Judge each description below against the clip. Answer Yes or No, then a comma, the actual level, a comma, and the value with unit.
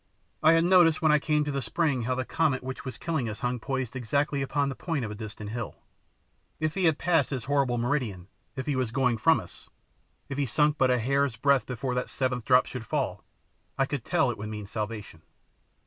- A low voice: Yes, low, 130 Hz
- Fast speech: Yes, fast, 225 wpm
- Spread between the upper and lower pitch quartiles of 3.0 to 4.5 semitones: Yes, average, 3.7 semitones